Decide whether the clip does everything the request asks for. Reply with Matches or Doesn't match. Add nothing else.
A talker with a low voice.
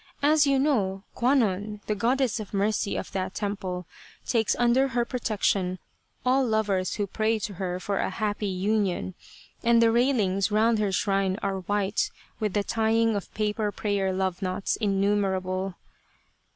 Doesn't match